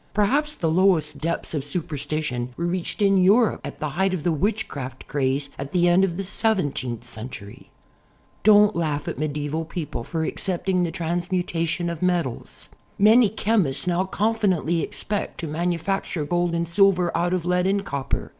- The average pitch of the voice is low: No, medium, 175 Hz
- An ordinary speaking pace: Yes, average, 170 wpm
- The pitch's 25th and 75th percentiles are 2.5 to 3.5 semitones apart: No, average, 4.1 semitones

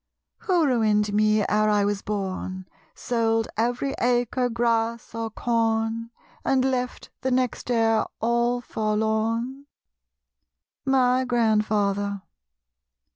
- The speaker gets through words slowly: Yes, slow, 100 wpm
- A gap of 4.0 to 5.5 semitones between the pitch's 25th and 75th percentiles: No, narrow, 2.5 semitones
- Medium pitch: No, high, 225 Hz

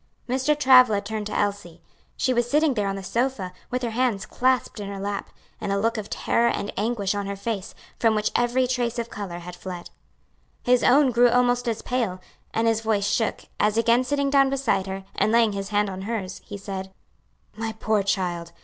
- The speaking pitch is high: Yes, high, 220 Hz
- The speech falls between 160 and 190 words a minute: No, fast, 205 wpm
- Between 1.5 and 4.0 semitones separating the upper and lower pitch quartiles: Yes, average, 3.7 semitones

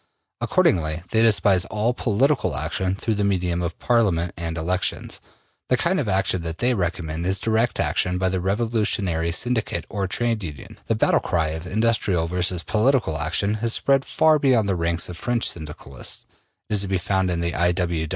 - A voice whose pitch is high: No, very low, 95 Hz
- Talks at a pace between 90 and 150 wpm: No, average, 180 wpm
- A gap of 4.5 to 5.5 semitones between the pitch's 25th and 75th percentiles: Yes, average, 4.8 semitones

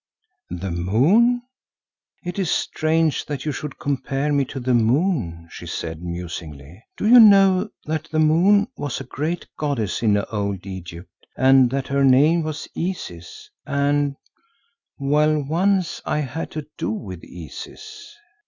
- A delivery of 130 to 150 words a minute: Yes, average, 140 wpm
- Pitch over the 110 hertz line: Yes, medium, 140 Hz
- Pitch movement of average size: No, wide, 7.6 semitones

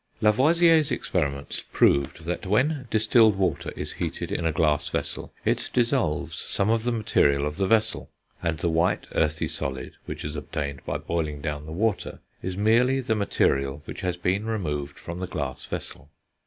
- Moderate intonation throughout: No, wide, 6.9 semitones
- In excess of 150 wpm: Yes, average, 170 wpm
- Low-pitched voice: Yes, very low, 90 Hz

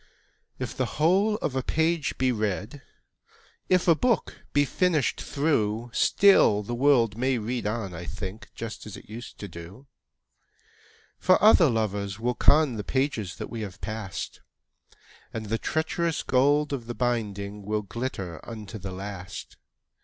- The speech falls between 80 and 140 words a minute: No, average, 155 wpm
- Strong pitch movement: Yes, wide, 5.7 semitones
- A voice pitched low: Yes, low, 115 Hz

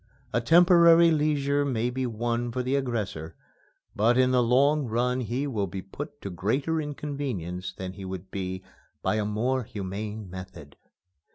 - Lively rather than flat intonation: Yes, wide, 5.9 semitones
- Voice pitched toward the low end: Yes, low, 120 Hz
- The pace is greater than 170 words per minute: No, average, 160 wpm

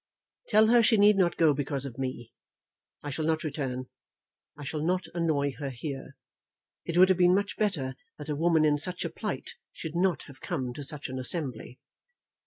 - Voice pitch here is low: No, medium, 150 Hz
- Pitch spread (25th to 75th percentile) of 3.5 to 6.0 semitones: Yes, average, 4.6 semitones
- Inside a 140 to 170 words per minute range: No, average, 195 wpm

